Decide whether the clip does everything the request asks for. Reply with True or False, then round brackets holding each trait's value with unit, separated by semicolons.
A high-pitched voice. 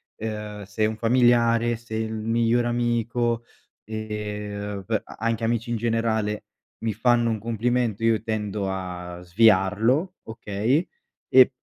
False (110 Hz)